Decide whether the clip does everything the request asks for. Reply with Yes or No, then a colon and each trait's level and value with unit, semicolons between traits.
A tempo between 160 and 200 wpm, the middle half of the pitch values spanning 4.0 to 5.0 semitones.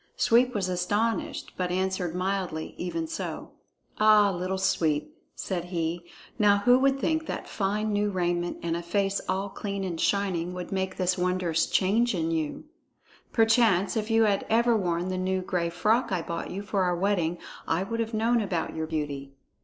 No: average, 180 wpm; average, 3.4 semitones